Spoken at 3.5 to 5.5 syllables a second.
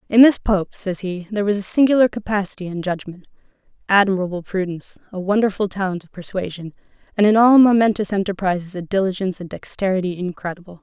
No: 6.5 syllables/s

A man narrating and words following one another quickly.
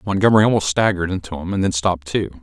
Yes: male; fast, 225 wpm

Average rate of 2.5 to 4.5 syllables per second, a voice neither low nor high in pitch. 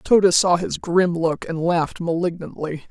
Yes: 4.2 syllables/s; medium, 170 Hz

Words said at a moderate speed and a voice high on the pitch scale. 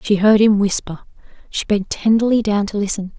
Yes: average, 190 wpm; high, 205 Hz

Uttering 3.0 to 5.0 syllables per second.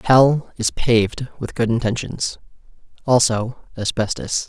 Yes: 4.2 syllables/s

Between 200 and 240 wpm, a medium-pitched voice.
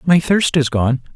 Yes: fast, 205 wpm; medium, 150 Hz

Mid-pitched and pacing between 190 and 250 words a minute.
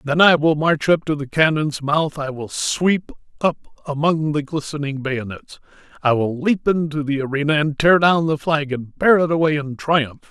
Yes: medium, 150 Hz; average, 200 wpm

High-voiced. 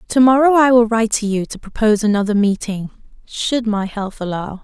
Yes: high, 220 Hz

